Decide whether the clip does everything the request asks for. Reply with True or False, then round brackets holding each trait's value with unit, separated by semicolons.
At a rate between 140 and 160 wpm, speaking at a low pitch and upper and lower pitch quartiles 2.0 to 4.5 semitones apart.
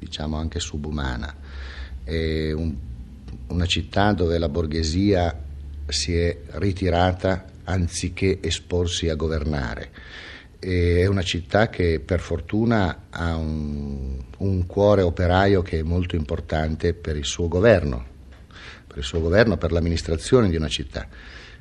False (125 wpm; 85 Hz; 3.1 semitones)